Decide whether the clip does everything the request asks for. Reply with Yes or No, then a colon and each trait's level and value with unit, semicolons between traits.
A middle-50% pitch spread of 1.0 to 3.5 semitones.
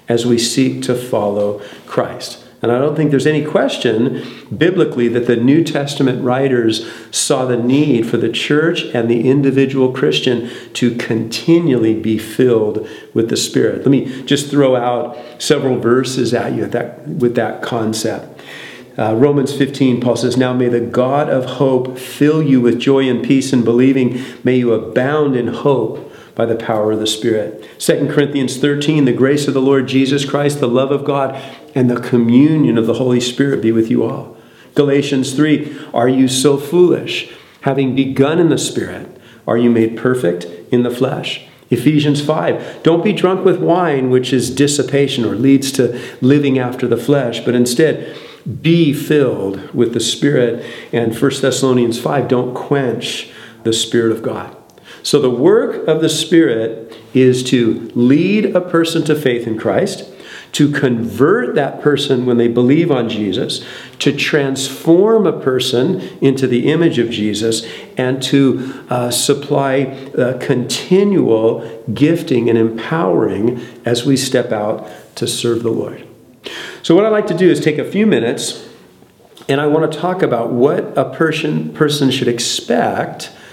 Yes: average, 3.2 semitones